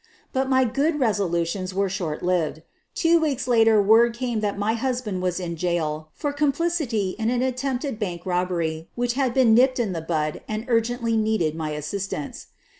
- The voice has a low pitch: No, high, 220 Hz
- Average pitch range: No, wide, 6.1 semitones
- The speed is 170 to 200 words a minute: Yes, average, 175 wpm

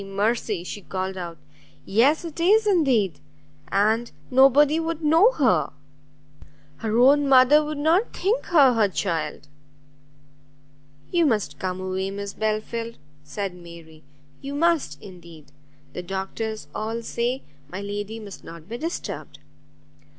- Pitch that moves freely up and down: Yes, wide, 7.2 semitones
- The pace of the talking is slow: Yes, slow, 130 wpm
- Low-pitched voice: No, high, 220 Hz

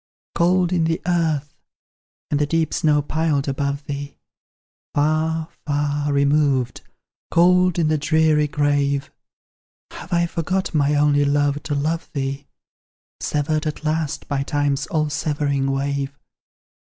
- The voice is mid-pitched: Yes, medium, 150 Hz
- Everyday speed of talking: No, slow, 125 wpm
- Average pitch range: No, narrow, 2.1 semitones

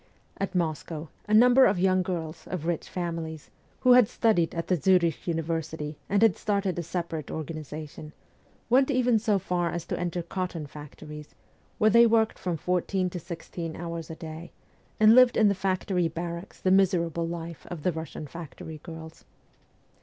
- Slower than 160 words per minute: No, average, 170 wpm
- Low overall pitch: No, medium, 170 Hz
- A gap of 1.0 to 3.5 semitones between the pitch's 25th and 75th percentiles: Yes, average, 3.0 semitones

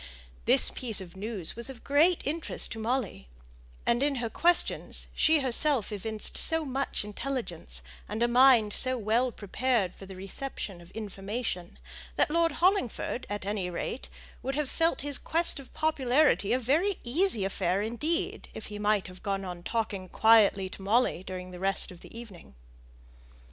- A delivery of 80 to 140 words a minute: No, average, 165 wpm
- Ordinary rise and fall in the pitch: No, wide, 5.8 semitones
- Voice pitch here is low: No, high, 230 Hz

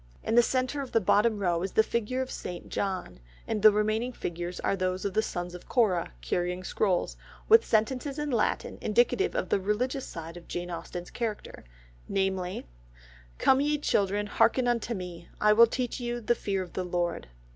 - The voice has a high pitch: Yes, high, 210 Hz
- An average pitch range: Yes, average, 4.9 semitones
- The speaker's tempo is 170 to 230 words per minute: Yes, average, 190 wpm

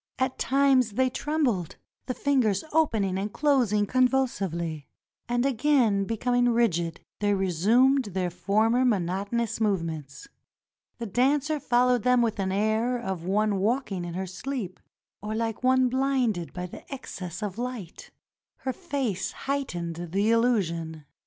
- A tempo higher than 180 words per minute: No, slow, 135 wpm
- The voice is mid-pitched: No, high, 220 Hz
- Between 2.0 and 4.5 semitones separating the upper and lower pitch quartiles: No, average, 5.2 semitones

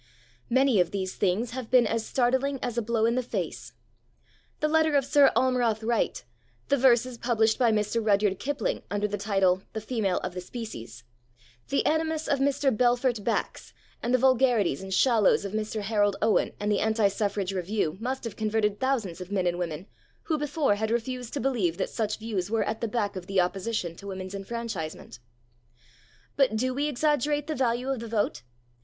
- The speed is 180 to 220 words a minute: Yes, average, 190 wpm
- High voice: Yes, high, 225 Hz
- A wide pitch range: No, average, 4.3 semitones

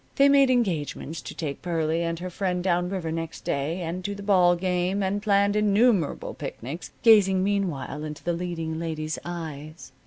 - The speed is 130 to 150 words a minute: No, average, 175 wpm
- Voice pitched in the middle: Yes, medium, 175 Hz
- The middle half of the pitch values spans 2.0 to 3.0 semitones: No, average, 3.5 semitones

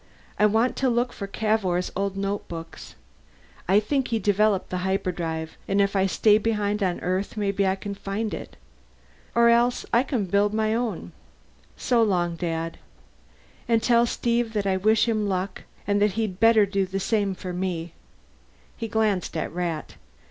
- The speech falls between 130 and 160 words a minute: No, average, 170 wpm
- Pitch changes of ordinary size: Yes, average, 3.0 semitones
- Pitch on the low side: No, high, 200 Hz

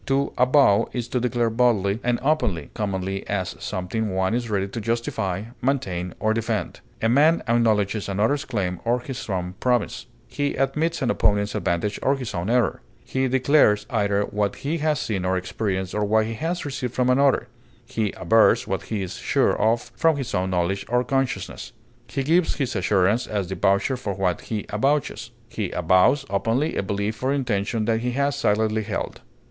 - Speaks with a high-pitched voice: No, low, 110 Hz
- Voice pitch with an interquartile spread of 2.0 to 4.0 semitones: No, average, 4.7 semitones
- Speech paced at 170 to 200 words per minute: Yes, average, 180 wpm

